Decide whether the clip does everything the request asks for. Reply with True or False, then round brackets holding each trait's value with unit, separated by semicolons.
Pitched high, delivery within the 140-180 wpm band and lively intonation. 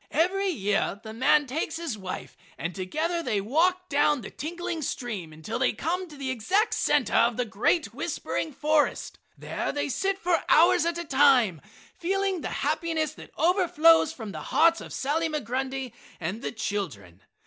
True (295 Hz; 170 wpm; 7.2 semitones)